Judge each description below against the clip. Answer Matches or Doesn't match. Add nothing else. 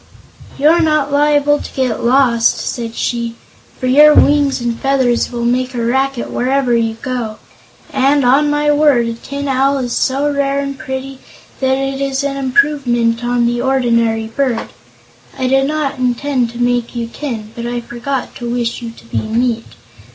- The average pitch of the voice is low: Doesn't match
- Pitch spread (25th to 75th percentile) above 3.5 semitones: Doesn't match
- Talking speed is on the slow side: Doesn't match